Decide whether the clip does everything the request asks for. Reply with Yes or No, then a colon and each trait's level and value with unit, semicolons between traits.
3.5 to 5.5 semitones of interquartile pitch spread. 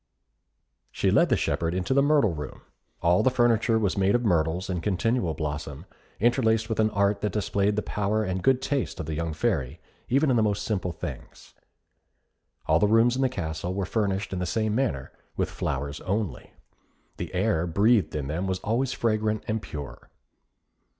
Yes: average, 4.9 semitones